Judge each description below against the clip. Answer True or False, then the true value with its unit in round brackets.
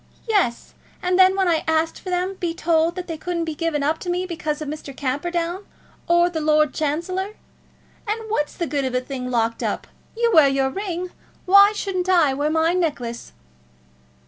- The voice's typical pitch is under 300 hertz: False (330 Hz)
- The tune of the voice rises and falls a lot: False (3.6 semitones)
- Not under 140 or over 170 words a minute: False (190 wpm)